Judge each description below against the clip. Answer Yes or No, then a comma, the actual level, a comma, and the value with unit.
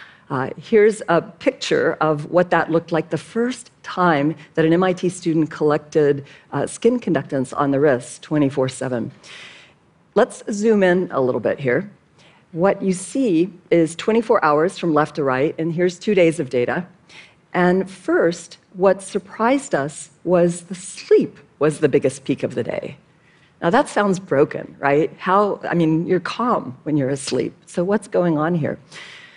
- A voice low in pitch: No, medium, 170 Hz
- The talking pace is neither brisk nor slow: Yes, average, 165 wpm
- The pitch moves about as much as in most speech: Yes, average, 3.9 semitones